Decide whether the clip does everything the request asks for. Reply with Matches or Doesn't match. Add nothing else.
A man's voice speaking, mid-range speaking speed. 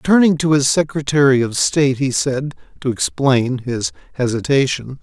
Matches